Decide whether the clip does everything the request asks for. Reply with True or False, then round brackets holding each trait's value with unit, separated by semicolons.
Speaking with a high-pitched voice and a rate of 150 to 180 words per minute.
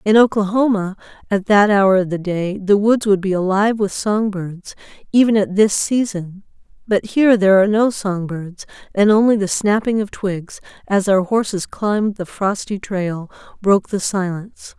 True (200 Hz; 175 wpm)